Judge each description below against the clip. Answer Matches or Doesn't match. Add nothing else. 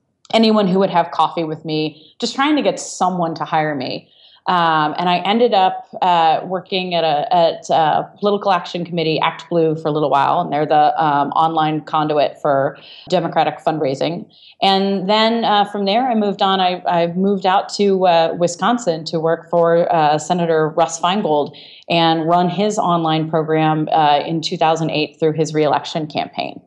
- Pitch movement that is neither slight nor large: Matches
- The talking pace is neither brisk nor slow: Matches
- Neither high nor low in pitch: Matches